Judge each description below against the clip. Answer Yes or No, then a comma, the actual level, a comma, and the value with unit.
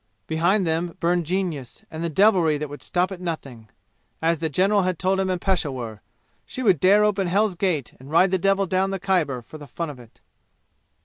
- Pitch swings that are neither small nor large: Yes, average, 3.9 semitones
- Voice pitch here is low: No, medium, 175 Hz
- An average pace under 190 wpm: No, fast, 205 wpm